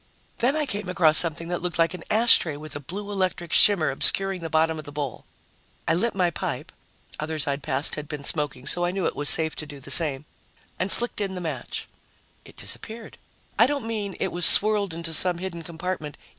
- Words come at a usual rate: No, fast, 210 wpm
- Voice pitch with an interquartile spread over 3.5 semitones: Yes, average, 4.1 semitones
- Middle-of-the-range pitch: Yes, medium, 170 Hz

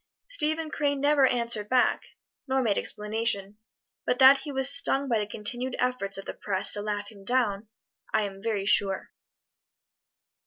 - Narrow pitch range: No, average, 4.5 semitones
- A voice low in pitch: No, high, 230 Hz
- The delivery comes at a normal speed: Yes, average, 160 wpm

